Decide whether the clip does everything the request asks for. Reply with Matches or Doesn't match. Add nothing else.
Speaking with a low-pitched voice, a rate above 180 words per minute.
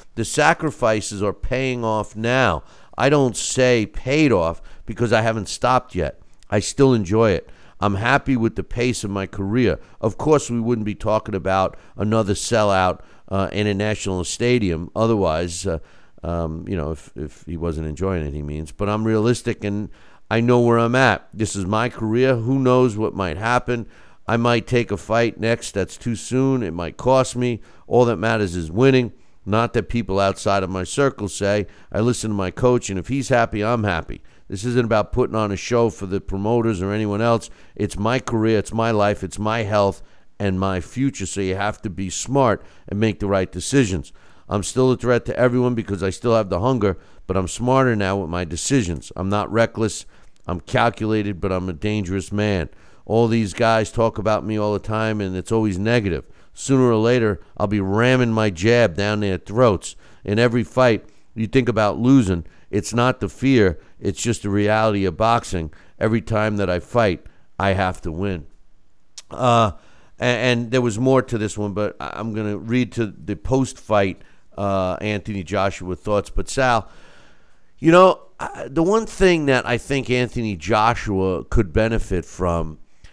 Matches